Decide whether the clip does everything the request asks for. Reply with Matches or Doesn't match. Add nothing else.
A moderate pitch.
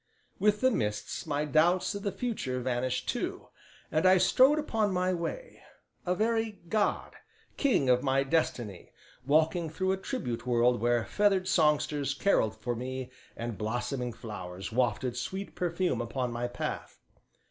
Matches